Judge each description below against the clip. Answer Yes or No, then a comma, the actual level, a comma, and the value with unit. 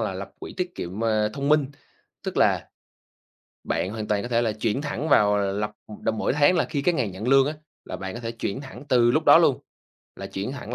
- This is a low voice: Yes, low, 120 Hz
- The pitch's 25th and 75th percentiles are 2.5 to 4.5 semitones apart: No, average, 4.9 semitones